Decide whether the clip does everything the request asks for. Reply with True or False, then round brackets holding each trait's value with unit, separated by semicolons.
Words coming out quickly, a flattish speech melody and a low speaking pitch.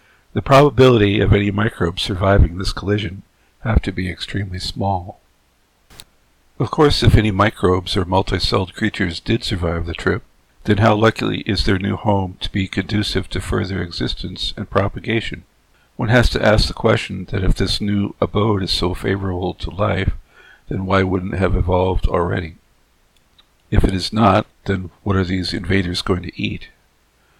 False (165 wpm; 2.3 semitones; 95 Hz)